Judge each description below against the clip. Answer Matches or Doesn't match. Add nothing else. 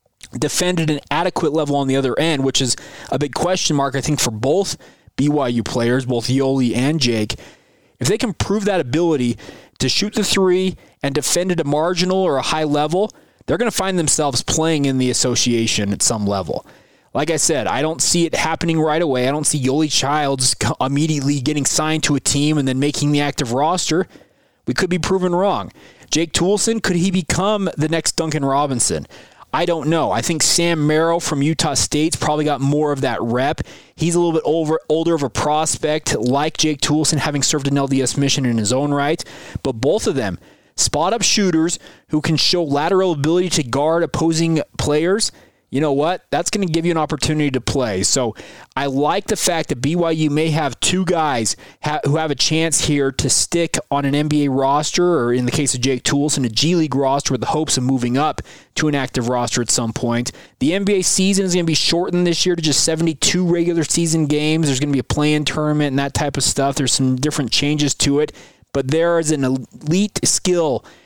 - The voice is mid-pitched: Matches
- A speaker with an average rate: Doesn't match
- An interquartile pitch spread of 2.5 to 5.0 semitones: Matches